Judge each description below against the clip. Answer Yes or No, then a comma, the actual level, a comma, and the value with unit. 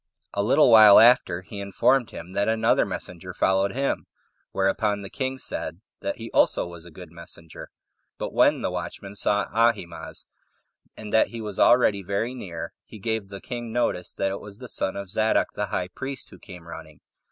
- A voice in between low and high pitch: No, low, 100 Hz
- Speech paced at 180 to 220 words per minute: Yes, average, 185 wpm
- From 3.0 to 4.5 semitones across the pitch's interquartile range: Yes, average, 3.4 semitones